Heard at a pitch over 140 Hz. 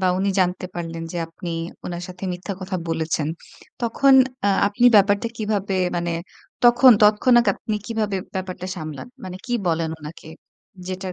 Yes: medium, 185 Hz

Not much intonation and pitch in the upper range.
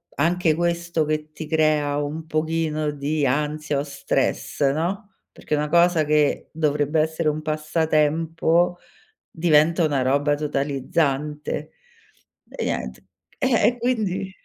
No: narrow, 2.0 semitones; medium, 155 Hz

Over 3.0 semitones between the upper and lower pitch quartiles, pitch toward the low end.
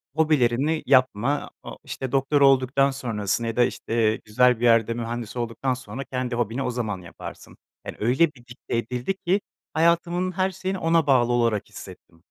Yes: average, 3.7 semitones; low, 125 Hz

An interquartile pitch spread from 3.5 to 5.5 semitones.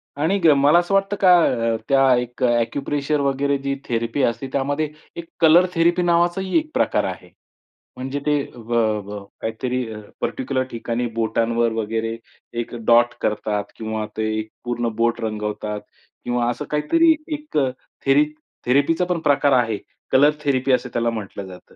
Yes: average, 4.5 semitones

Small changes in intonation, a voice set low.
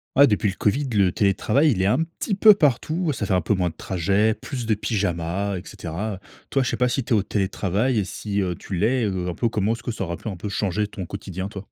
No: average, 3.9 semitones; low, 105 Hz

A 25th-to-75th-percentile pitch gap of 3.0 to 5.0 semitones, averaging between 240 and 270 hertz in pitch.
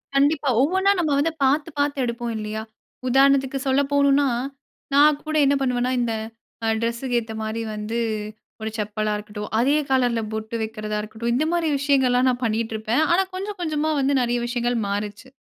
Yes: average, 4.2 semitones; very high, 250 Hz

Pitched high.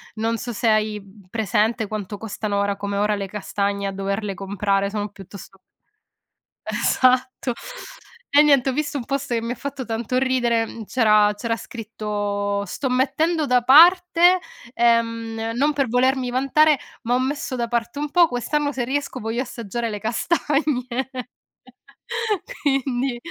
Yes: high, 235 Hz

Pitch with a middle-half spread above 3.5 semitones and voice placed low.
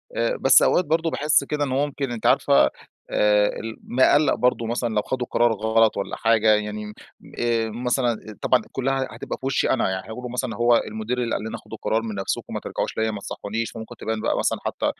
No: average, 2.8 semitones; low, 115 Hz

